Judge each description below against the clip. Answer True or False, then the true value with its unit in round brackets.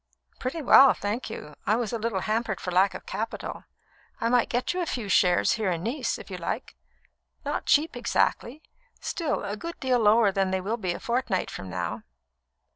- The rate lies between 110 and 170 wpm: False (200 wpm)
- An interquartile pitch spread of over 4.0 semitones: True (4.5 semitones)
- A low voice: False (225 Hz)